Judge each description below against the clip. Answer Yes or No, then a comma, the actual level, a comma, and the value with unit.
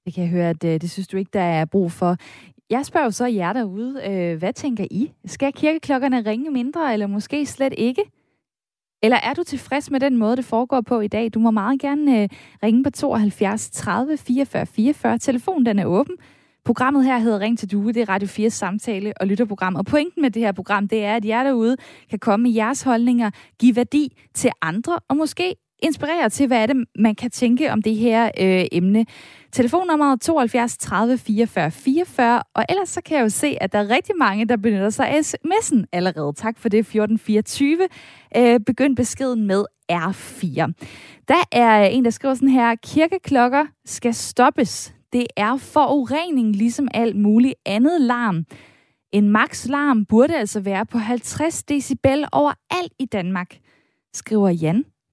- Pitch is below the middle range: No, high, 235 Hz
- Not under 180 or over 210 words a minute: Yes, average, 185 wpm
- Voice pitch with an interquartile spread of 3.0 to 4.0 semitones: No, average, 4.7 semitones